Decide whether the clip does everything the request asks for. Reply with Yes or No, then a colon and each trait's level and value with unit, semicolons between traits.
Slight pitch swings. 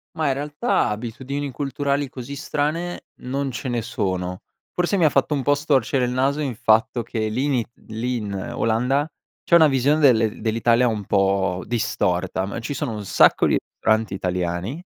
No: average, 4.7 semitones